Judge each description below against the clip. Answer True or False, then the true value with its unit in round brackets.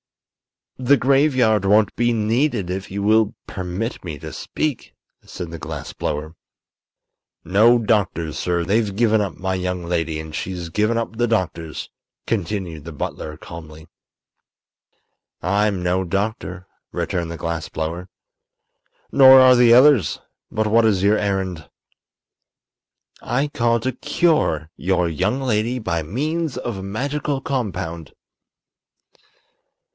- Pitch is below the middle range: True (100 Hz)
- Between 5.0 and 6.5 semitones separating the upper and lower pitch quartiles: True (5.5 semitones)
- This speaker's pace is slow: True (130 wpm)